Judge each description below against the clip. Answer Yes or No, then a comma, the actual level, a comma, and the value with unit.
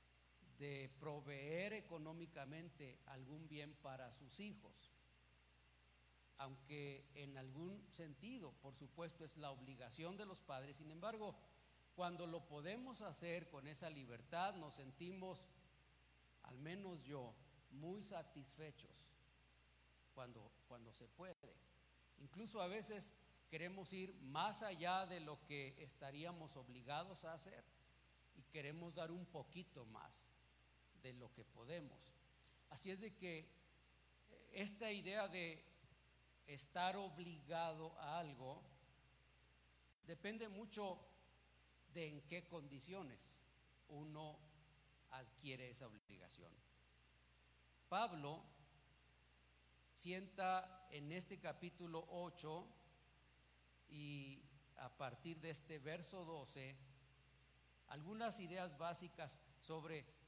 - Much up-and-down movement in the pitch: Yes, wide, 7.1 semitones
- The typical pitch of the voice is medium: Yes, medium, 145 Hz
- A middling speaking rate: No, slow, 100 wpm